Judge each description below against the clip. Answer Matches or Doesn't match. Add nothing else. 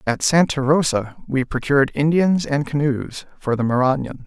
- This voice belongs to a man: Matches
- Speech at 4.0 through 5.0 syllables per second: Matches